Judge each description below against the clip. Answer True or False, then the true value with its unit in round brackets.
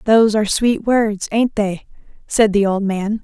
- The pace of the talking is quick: False (185 wpm)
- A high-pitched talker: True (210 Hz)